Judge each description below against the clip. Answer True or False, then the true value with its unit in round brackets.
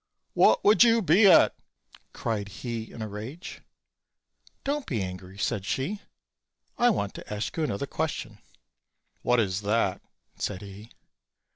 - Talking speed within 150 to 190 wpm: False (140 wpm)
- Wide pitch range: True (8.1 semitones)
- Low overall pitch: True (110 Hz)